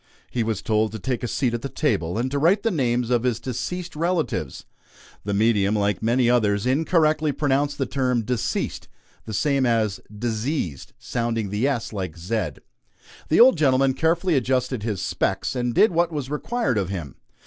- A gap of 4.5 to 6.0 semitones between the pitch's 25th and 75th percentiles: Yes, average, 4.9 semitones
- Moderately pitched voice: No, low, 125 Hz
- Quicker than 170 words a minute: Yes, average, 180 wpm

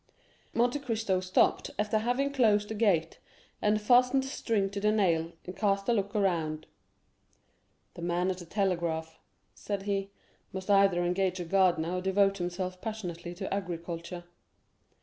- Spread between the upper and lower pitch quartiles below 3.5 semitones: Yes, average, 3.1 semitones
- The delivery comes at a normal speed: Yes, average, 150 wpm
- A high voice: Yes, high, 195 Hz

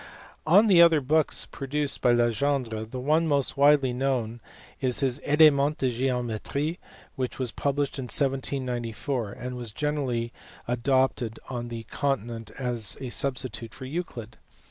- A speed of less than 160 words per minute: Yes, average, 145 wpm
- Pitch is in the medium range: No, low, 130 Hz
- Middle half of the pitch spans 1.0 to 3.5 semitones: Yes, average, 3.1 semitones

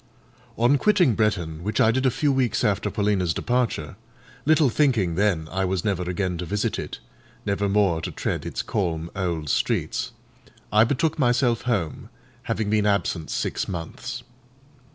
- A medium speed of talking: Yes, average, 150 wpm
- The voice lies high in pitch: No, low, 105 Hz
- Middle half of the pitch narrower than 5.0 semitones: No, average, 5.3 semitones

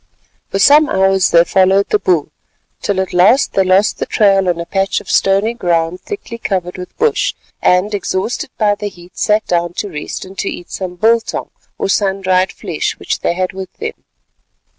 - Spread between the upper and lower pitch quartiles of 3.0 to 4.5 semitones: No, narrow, 2.4 semitones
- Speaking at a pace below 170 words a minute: No, average, 190 wpm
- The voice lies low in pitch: No, high, 190 Hz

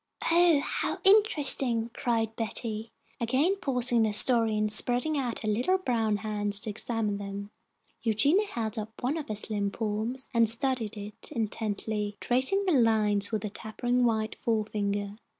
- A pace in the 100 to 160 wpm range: Yes, average, 155 wpm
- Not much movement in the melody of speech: No, average, 3.0 semitones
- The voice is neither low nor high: No, high, 225 Hz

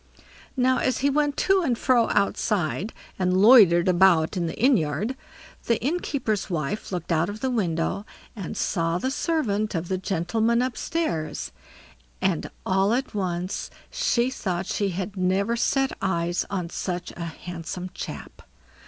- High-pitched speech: Yes, high, 195 Hz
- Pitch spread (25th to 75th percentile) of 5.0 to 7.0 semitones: Yes, wide, 5.4 semitones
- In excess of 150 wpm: No, average, 145 wpm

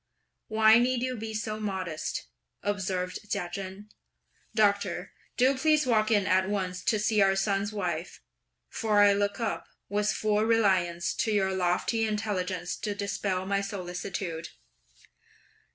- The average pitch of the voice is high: Yes, high, 200 Hz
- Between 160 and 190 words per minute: No, slow, 135 wpm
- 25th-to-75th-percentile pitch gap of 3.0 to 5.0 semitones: No, narrow, 2.5 semitones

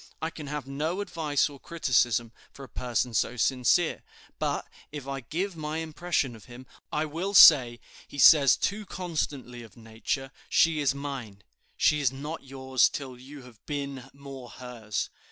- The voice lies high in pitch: No, medium, 140 Hz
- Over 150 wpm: Yes, average, 165 wpm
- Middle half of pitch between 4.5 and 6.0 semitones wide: No, average, 3.6 semitones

